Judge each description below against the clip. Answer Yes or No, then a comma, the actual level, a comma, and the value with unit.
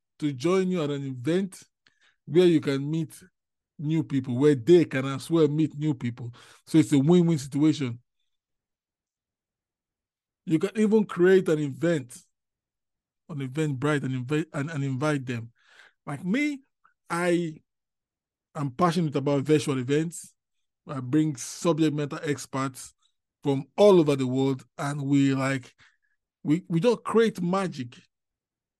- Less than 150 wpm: Yes, average, 140 wpm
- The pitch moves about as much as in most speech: Yes, average, 4.1 semitones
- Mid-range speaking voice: Yes, medium, 145 Hz